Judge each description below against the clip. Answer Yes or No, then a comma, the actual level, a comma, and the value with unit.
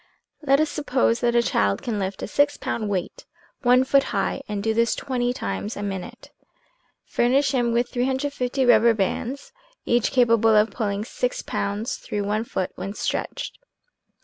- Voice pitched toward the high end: Yes, high, 235 Hz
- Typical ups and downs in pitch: Yes, average, 3.7 semitones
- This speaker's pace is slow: No, average, 165 wpm